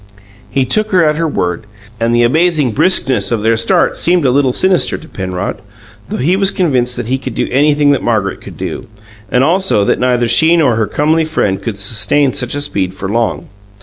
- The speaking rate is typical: No, fast, 210 wpm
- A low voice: Yes, low, 130 Hz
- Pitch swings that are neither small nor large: No, wide, 5.9 semitones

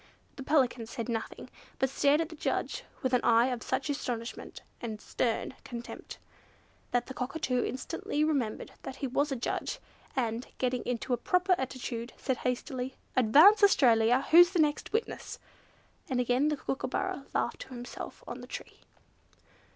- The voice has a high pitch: Yes, very high, 255 Hz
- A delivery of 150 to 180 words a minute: Yes, average, 160 wpm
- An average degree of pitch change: Yes, average, 3.4 semitones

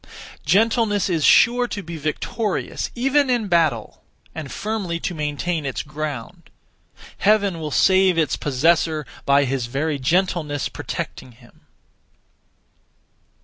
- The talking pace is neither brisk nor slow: No, slow, 115 wpm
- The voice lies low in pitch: No, medium, 165 Hz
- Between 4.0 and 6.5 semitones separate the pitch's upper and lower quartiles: Yes, wide, 5.6 semitones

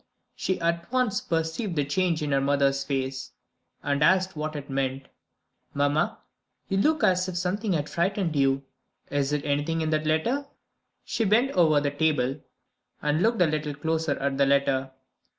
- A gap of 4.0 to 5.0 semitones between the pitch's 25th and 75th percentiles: Yes, average, 4.5 semitones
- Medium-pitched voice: Yes, medium, 155 Hz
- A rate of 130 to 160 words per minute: No, average, 170 wpm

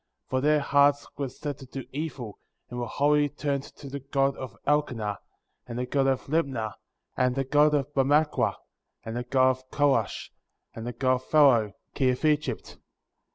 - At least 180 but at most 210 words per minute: Yes, average, 185 wpm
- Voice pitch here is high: No, low, 135 Hz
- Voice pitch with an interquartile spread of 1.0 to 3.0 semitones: Yes, narrow, 2.5 semitones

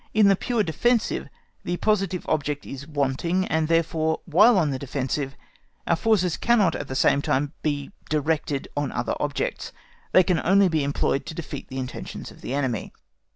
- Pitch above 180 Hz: No, medium, 160 Hz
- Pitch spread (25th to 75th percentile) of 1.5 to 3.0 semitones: No, average, 4.6 semitones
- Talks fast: No, average, 175 wpm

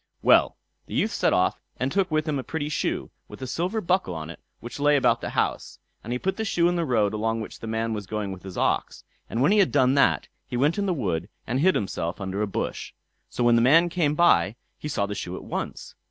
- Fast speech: Yes, fast, 255 wpm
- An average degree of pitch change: No, wide, 7.6 semitones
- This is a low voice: Yes, low, 130 Hz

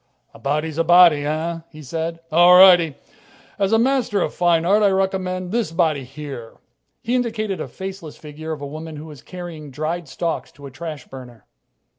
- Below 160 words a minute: No, average, 185 wpm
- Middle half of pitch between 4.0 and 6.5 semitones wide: No, average, 3.5 semitones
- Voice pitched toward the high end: No, medium, 165 Hz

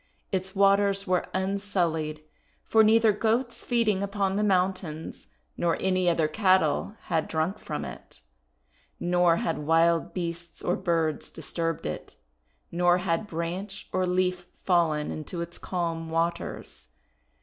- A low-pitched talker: No, medium, 180 Hz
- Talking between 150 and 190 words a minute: No, slow, 135 wpm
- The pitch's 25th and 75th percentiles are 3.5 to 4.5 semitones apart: No, average, 2.9 semitones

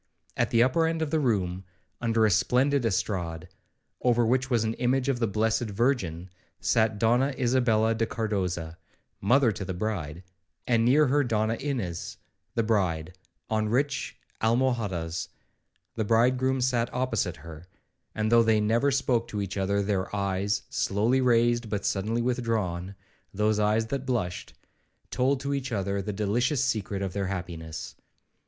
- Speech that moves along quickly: No, average, 155 wpm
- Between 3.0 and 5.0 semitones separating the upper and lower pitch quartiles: Yes, average, 4.1 semitones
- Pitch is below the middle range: Yes, low, 110 Hz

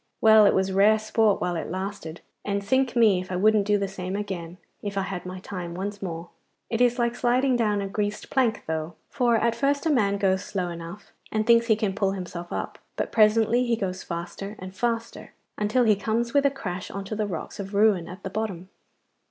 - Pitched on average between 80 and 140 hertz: No, high, 205 Hz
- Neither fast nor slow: No, fast, 220 wpm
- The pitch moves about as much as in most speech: Yes, average, 3.3 semitones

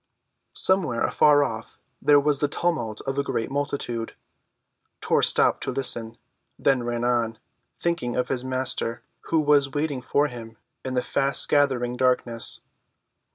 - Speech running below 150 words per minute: Yes, average, 140 wpm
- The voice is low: Yes, low, 130 Hz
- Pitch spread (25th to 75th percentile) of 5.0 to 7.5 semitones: No, average, 3.2 semitones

